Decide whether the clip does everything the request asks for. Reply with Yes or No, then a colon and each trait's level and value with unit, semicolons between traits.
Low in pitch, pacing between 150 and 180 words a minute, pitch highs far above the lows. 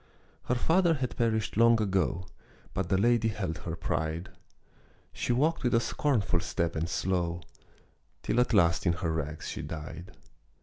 Yes: very low, 95 Hz; average, 160 wpm; wide, 5.8 semitones